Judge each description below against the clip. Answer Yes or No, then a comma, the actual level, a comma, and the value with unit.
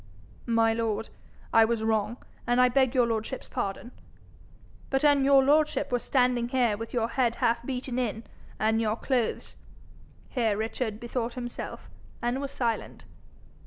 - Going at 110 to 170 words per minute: Yes, average, 155 wpm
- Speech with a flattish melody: Yes, narrow, 2.3 semitones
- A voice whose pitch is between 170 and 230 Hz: No, high, 240 Hz